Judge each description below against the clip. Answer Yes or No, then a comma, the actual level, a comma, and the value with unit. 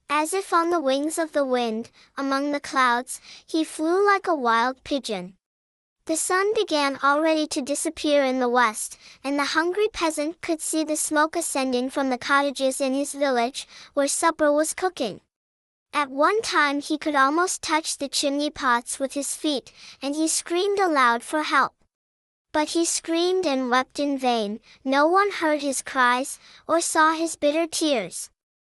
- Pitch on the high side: Yes, very high, 290 Hz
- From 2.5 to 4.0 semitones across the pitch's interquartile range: Yes, average, 3.2 semitones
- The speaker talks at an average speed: Yes, average, 170 wpm